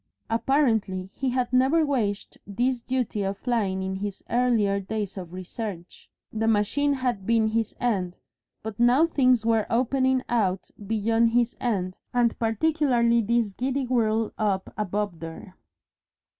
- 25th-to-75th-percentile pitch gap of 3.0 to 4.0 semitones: Yes, average, 3.7 semitones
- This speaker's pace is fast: No, average, 140 wpm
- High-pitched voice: Yes, high, 225 Hz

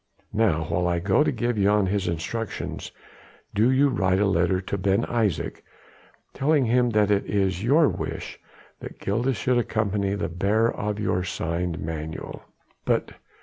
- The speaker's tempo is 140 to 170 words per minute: Yes, average, 155 wpm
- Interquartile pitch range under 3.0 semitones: No, average, 4.1 semitones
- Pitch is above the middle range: No, low, 100 Hz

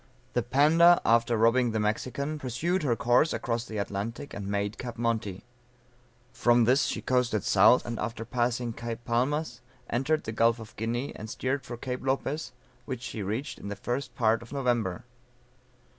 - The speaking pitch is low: Yes, low, 120 Hz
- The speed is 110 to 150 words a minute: No, average, 170 wpm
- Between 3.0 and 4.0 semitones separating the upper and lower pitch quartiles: No, narrow, 2.6 semitones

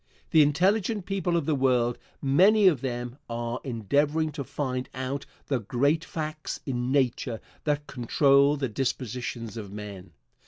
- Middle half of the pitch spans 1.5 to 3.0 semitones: No, average, 4.0 semitones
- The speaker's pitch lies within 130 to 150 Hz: Yes, low, 135 Hz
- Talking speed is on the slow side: No, average, 145 wpm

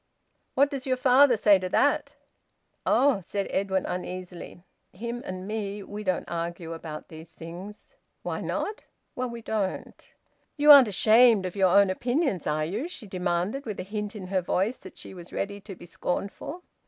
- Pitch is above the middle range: Yes, high, 200 Hz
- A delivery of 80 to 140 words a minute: No, average, 175 wpm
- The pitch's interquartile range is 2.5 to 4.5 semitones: No, average, 4.9 semitones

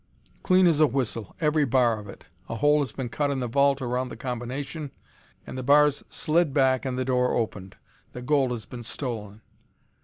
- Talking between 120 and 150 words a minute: No, average, 195 wpm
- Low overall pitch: Yes, low, 130 Hz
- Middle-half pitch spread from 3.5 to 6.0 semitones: No, average, 3.1 semitones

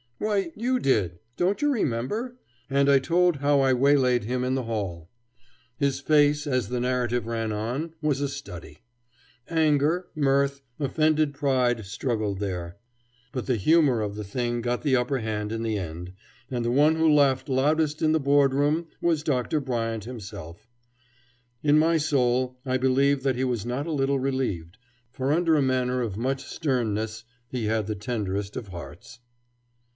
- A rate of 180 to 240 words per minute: No, average, 170 wpm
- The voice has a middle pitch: No, low, 130 Hz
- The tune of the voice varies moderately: Yes, average, 4.4 semitones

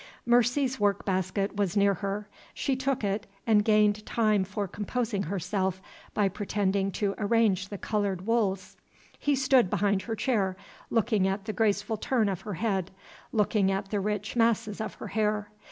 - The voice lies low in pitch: No, high, 205 Hz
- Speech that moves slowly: No, average, 165 wpm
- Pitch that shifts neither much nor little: No, narrow, 2.3 semitones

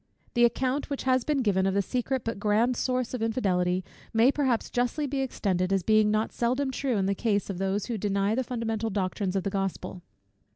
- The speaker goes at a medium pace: No, fast, 210 wpm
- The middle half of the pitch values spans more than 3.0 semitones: Yes, average, 4.4 semitones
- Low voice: No, high, 225 Hz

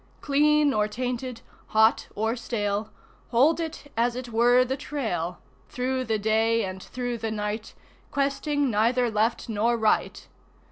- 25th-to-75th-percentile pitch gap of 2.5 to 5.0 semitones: Yes, average, 2.9 semitones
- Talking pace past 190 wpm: No, average, 140 wpm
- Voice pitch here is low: No, high, 235 Hz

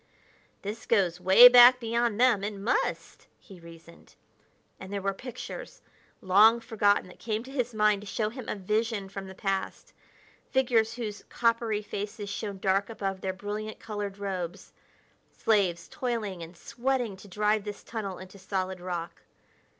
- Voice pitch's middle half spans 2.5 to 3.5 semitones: Yes, average, 3.0 semitones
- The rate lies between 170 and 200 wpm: No, average, 155 wpm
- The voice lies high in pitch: Yes, high, 205 Hz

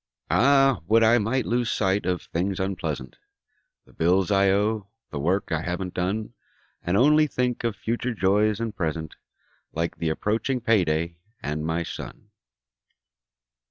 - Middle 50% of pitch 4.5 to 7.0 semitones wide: Yes, average, 4.9 semitones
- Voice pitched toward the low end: Yes, low, 100 Hz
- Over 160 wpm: No, average, 145 wpm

